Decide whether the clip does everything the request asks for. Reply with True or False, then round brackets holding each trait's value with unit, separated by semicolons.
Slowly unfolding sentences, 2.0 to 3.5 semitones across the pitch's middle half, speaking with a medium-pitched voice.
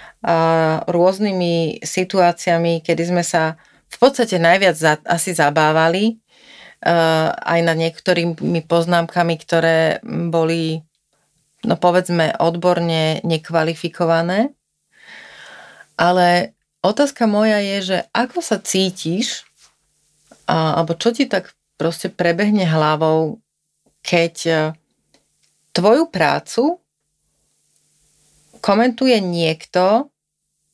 True (80 wpm; 2.6 semitones; 170 Hz)